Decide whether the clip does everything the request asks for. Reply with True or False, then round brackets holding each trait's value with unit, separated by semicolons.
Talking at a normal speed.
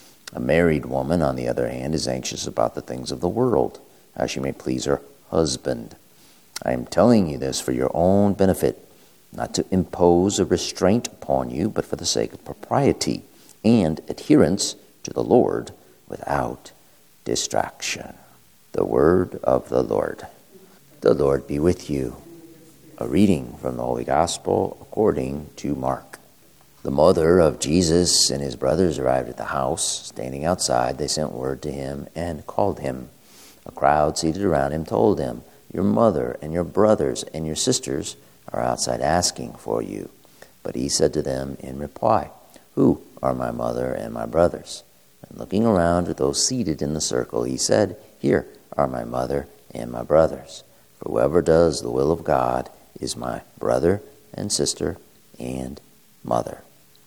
True (165 wpm)